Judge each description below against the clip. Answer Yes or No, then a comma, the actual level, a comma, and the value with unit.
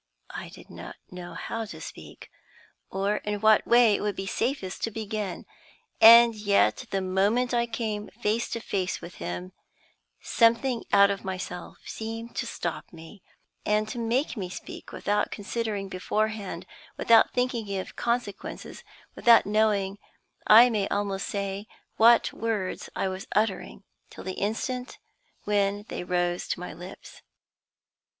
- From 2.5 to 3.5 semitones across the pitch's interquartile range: Yes, average, 2.9 semitones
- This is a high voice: Yes, high, 210 Hz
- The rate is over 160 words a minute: No, average, 145 wpm